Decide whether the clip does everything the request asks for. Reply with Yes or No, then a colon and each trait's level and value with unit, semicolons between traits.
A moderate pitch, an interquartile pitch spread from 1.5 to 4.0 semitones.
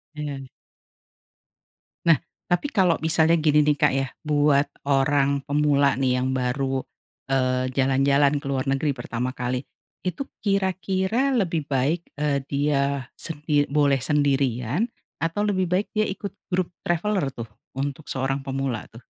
Yes: medium, 145 Hz; average, 3.7 semitones